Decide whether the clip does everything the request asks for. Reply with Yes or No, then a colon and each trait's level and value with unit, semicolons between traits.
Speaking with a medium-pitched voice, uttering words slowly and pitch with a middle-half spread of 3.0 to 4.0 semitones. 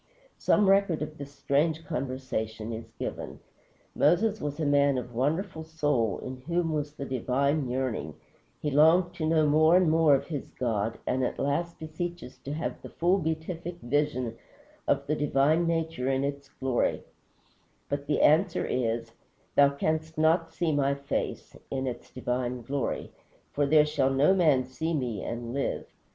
No: medium, 145 Hz; average, 165 wpm; average, 3.6 semitones